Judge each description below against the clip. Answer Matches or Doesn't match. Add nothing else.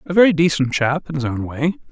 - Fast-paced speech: Matches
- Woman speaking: Doesn't match